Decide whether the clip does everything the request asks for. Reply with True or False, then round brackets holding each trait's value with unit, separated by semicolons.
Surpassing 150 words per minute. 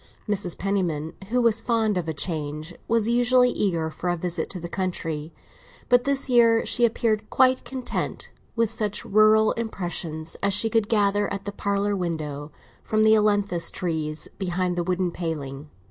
True (165 wpm)